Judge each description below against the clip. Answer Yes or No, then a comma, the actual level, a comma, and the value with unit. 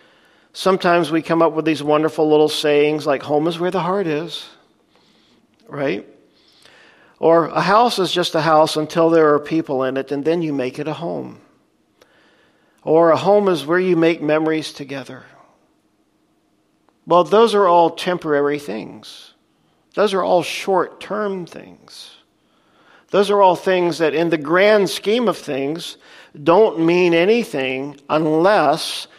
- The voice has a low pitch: No, medium, 165 Hz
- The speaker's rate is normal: Yes, average, 150 wpm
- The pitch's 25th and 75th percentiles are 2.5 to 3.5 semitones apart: Yes, average, 3.0 semitones